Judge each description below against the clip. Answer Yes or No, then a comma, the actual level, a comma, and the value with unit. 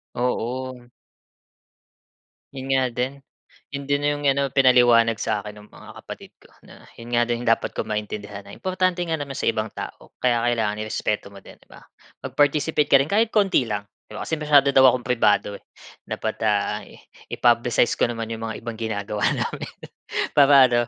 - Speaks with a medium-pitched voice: No, low, 120 Hz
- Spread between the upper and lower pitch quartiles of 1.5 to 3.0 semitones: No, average, 4.2 semitones